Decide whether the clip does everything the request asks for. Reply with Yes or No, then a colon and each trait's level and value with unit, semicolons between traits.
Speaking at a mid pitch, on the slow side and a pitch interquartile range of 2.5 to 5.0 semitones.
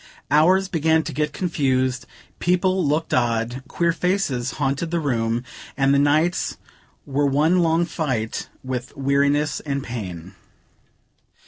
Yes: medium, 145 Hz; slow, 125 wpm; average, 4.2 semitones